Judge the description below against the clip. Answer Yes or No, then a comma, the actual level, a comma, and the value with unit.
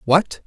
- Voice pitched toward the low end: No, medium, 160 Hz